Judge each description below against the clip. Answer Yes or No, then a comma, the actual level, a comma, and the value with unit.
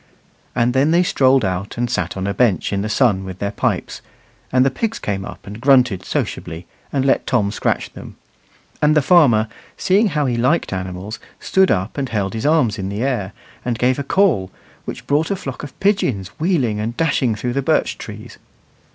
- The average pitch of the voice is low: Yes, low, 125 Hz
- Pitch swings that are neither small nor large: No, wide, 6.1 semitones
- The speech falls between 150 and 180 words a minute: No, average, 200 wpm